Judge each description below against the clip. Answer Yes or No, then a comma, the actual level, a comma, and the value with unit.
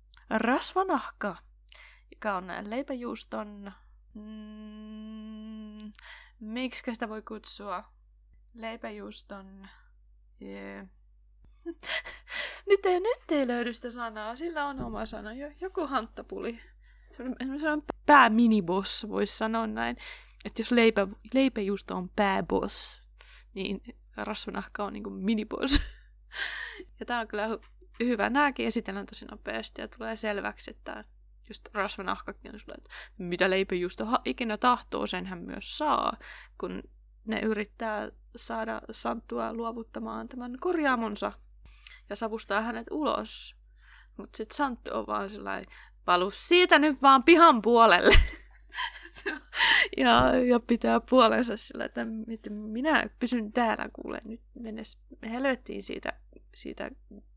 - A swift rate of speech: No, average, 110 wpm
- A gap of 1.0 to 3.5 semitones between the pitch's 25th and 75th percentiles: No, average, 3.9 semitones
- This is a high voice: Yes, high, 225 Hz